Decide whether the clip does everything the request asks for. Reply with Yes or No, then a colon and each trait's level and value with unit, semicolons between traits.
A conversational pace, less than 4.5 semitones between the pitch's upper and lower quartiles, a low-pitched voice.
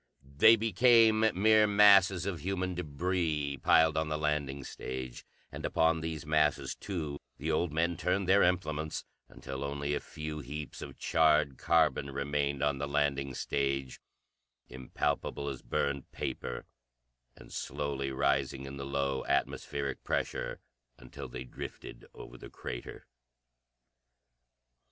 No: slow, 130 wpm; average, 3.8 semitones; very low, 75 Hz